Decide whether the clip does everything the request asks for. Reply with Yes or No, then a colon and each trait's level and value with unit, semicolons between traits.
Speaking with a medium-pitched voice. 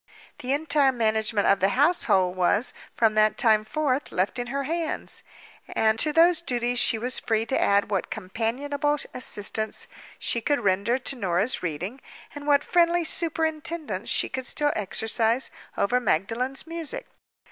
No: high, 245 Hz